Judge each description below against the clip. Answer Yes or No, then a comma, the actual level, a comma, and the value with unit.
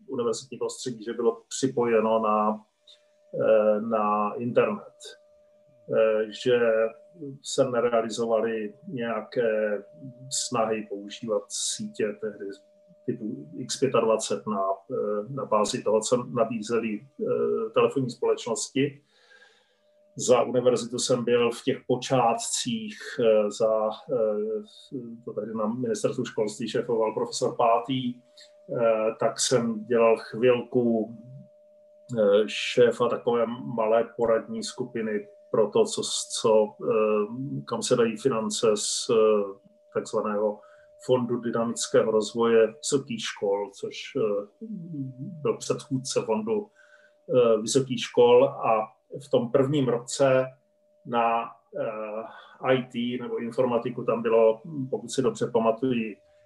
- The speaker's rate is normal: No, slow, 90 wpm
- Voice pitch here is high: No, low, 125 Hz